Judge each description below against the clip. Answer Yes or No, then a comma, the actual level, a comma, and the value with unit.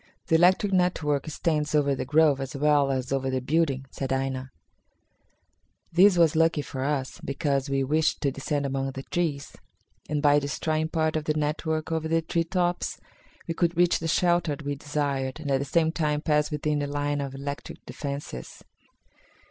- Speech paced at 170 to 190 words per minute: Yes, average, 180 wpm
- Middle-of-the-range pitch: Yes, medium, 150 Hz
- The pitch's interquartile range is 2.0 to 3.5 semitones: Yes, average, 2.7 semitones